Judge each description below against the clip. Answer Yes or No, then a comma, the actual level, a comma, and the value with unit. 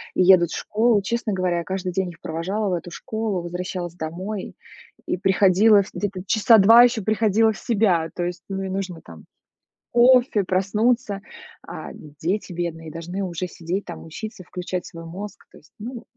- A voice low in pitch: No, high, 190 Hz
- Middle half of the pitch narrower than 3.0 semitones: No, average, 3.5 semitones